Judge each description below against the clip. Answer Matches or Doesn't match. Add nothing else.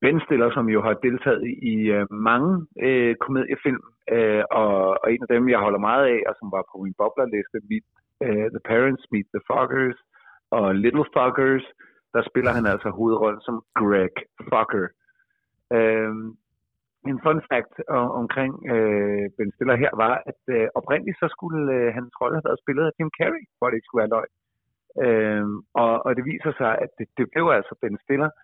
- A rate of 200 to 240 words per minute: Doesn't match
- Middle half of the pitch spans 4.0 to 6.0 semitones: Matches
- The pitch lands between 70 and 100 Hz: Doesn't match